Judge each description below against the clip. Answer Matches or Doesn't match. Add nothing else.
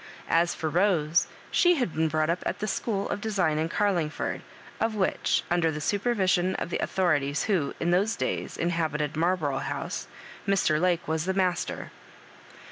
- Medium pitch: Matches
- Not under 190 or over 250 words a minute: Doesn't match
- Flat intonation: Doesn't match